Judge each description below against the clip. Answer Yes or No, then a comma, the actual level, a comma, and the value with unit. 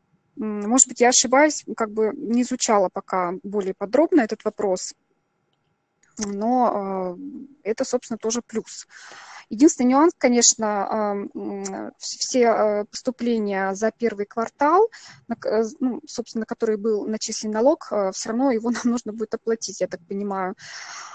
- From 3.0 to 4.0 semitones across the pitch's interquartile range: Yes, average, 3.4 semitones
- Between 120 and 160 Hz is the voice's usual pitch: No, high, 225 Hz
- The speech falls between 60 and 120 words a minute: Yes, average, 115 wpm